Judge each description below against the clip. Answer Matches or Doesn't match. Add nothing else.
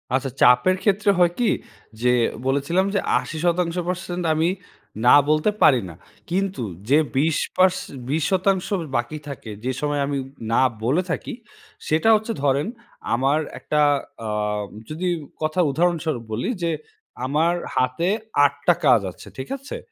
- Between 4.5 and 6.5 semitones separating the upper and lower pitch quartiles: Matches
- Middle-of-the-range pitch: Matches